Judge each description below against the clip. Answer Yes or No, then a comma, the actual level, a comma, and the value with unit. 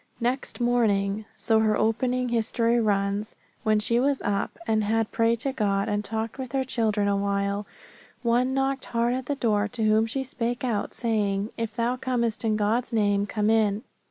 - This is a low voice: No, high, 225 Hz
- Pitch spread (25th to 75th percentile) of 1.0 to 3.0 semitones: Yes, average, 2.7 semitones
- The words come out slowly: No, average, 180 wpm